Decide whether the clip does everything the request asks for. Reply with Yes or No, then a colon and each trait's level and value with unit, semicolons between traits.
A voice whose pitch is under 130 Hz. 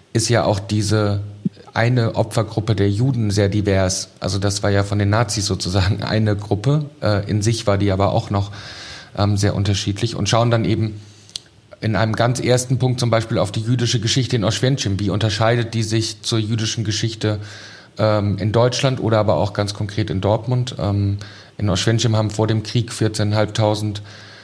Yes: low, 110 Hz